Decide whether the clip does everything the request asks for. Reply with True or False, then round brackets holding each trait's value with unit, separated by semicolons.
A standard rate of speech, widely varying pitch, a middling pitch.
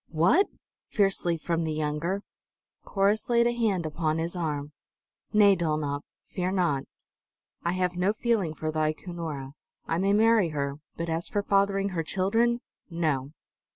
False (150 wpm; 4.3 semitones; 175 Hz)